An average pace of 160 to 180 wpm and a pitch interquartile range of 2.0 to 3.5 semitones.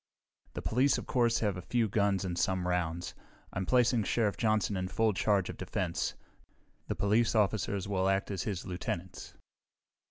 Yes: average, 165 wpm; average, 3.0 semitones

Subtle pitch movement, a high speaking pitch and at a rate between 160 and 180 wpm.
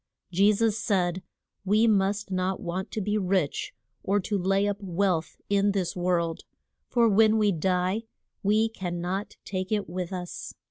Yes: narrow, 2.3 semitones; high, 195 Hz; average, 165 wpm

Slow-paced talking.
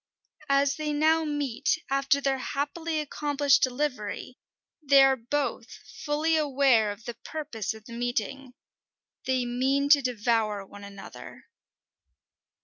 Yes: slow, 125 wpm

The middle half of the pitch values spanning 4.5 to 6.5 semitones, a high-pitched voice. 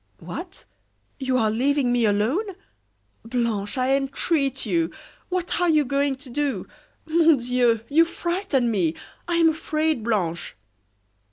Yes: wide, 5.6 semitones; very high, 265 Hz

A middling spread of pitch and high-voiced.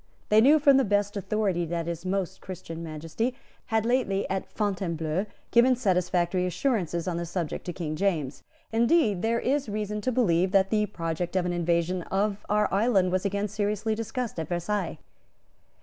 Yes: average, 3.7 semitones; high, 195 Hz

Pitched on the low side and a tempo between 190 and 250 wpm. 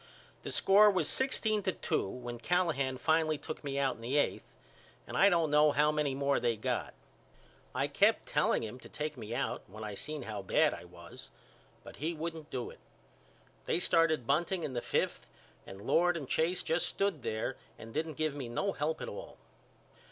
No: medium, 150 Hz; average, 195 wpm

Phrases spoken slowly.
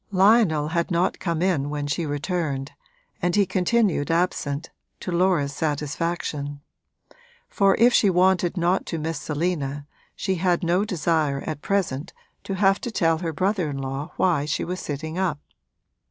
No: average, 155 wpm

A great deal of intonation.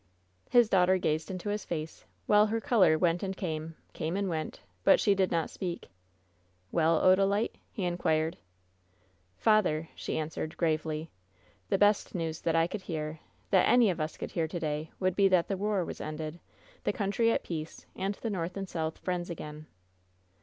No: average, 3.7 semitones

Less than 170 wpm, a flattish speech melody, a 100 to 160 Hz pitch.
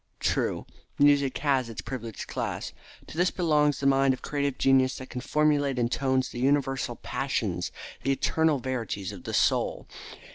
Yes: average, 160 wpm; narrow, 2.0 semitones; low, 135 Hz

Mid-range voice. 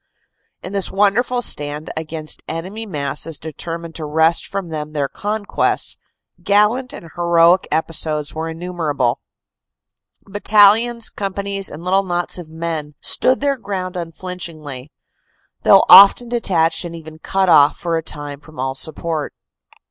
Yes: medium, 170 Hz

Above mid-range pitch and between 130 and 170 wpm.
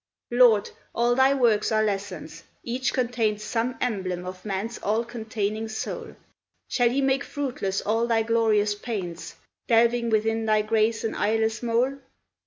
Yes: high, 225 Hz; average, 145 wpm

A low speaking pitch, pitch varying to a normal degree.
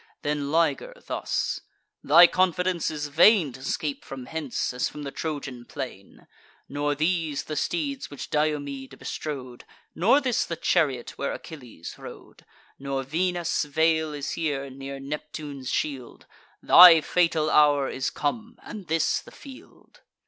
No: medium, 150 Hz; average, 3.4 semitones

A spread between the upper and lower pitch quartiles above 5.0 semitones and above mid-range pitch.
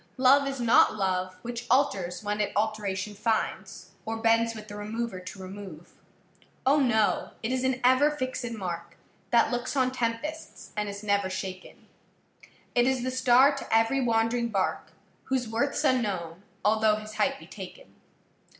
No: average, 4.1 semitones; high, 225 Hz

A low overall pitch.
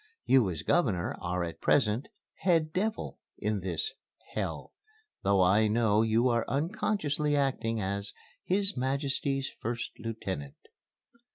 Yes: low, 115 Hz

